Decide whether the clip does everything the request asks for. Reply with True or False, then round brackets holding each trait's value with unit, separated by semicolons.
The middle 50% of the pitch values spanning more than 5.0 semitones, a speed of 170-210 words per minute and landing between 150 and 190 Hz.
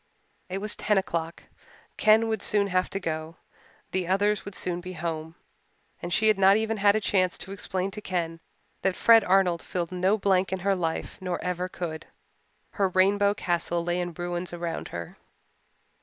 False (2.5 semitones; 180 wpm; 185 Hz)